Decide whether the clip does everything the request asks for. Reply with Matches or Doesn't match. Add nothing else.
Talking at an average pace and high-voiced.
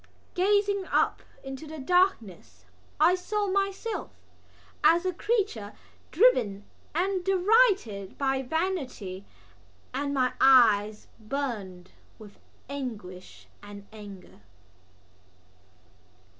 Doesn't match